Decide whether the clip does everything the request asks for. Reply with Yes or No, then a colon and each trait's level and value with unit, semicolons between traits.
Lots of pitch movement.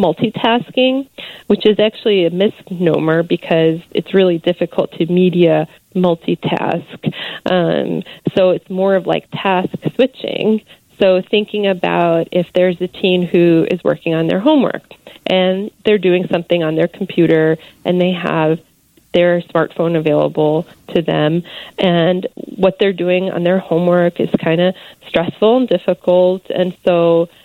No: narrow, 2.4 semitones